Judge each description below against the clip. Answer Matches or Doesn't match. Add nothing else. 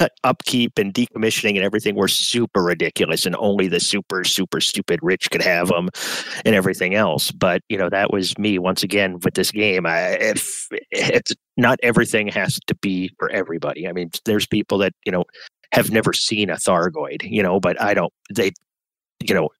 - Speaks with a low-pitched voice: Matches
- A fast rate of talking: Doesn't match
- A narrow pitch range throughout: Matches